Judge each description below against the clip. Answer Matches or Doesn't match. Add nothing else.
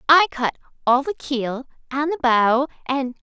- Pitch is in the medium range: Doesn't match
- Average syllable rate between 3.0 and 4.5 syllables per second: Matches